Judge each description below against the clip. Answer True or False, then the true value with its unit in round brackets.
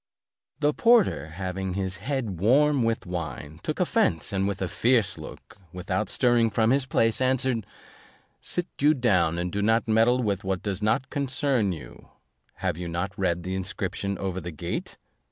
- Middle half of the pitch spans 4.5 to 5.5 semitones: True (5.2 semitones)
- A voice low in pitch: True (100 Hz)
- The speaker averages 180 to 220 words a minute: False (170 wpm)